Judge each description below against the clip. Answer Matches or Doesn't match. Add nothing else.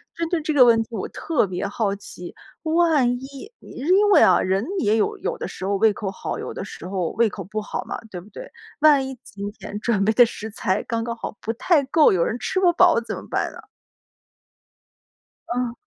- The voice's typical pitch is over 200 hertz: Matches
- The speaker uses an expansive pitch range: Matches